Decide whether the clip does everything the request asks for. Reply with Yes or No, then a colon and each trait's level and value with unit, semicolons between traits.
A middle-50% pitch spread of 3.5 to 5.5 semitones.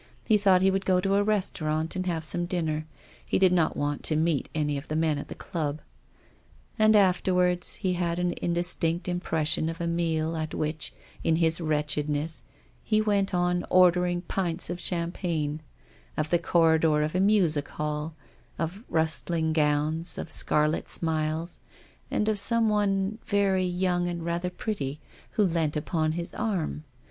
No: average, 2.7 semitones